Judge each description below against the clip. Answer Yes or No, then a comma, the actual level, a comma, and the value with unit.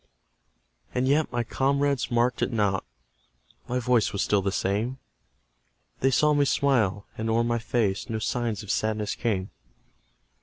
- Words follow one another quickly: No, average, 150 wpm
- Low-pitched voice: Yes, low, 120 Hz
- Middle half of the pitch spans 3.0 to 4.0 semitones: Yes, average, 3.4 semitones